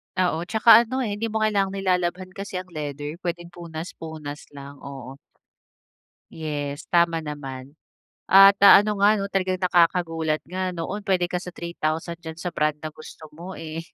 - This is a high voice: No, medium, 175 Hz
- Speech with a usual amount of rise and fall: Yes, average, 3.4 semitones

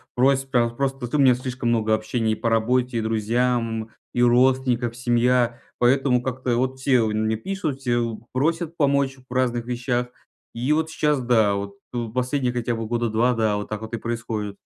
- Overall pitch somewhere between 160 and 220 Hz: No, low, 120 Hz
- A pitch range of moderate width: No, narrow, 2.3 semitones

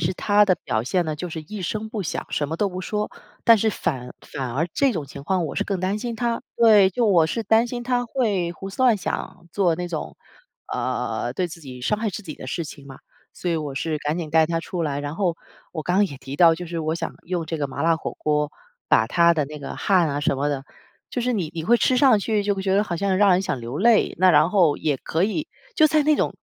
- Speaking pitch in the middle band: Yes, medium, 175 Hz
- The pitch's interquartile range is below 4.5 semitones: No, average, 5.1 semitones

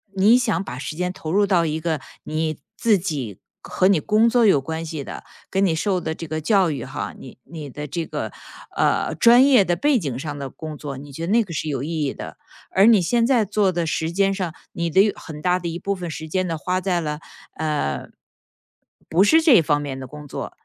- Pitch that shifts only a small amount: No, average, 4.6 semitones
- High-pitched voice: No, medium, 170 Hz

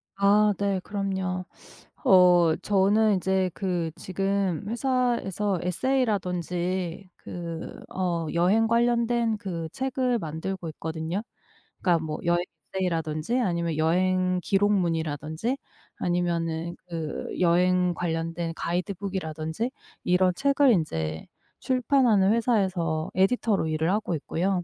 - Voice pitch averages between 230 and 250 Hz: No, medium, 185 Hz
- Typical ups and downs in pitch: Yes, average, 3.5 semitones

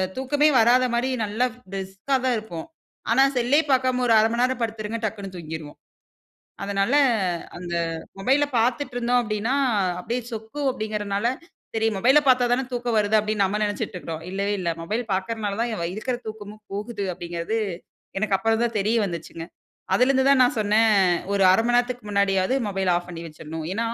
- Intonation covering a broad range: No, average, 3.9 semitones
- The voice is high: Yes, high, 215 Hz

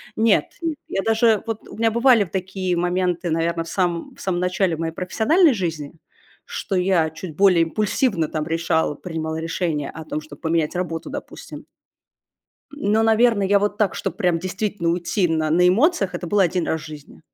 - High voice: No, medium, 180 Hz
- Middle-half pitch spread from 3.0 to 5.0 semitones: Yes, average, 4.0 semitones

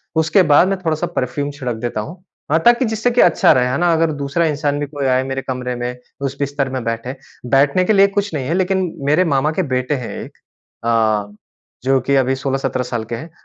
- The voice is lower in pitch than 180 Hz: Yes, medium, 140 Hz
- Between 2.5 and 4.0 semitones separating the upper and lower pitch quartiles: No, average, 4.4 semitones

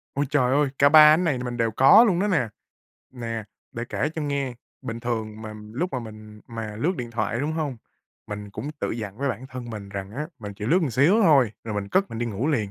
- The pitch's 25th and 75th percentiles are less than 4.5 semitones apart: No, average, 5.1 semitones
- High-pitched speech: No, low, 120 Hz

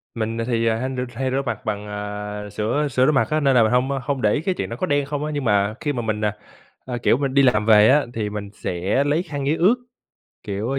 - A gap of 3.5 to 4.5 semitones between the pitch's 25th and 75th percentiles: No, average, 5.0 semitones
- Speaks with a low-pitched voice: Yes, low, 120 Hz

